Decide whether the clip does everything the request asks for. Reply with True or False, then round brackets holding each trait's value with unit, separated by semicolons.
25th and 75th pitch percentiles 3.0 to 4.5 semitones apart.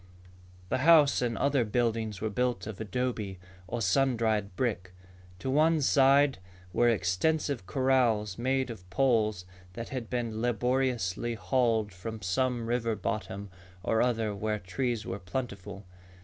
True (3.9 semitones)